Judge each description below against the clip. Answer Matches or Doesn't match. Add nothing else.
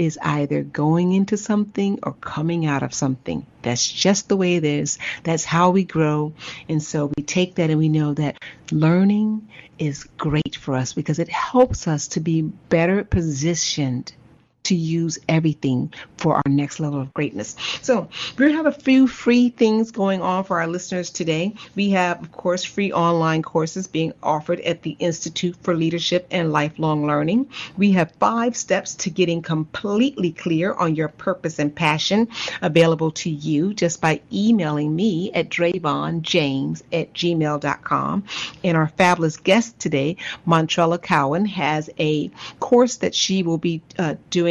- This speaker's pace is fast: Doesn't match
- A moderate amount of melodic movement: Matches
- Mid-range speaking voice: Matches